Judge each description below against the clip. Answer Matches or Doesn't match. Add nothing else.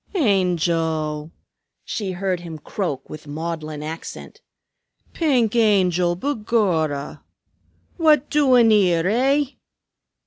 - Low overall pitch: Doesn't match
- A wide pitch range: Matches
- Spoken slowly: Matches